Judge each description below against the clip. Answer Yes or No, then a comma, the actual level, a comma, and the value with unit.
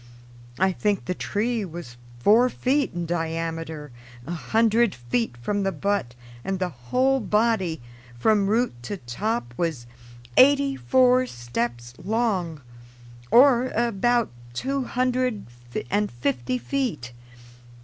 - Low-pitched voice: No, high, 200 Hz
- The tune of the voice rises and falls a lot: Yes, wide, 7.4 semitones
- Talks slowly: Yes, slow, 120 wpm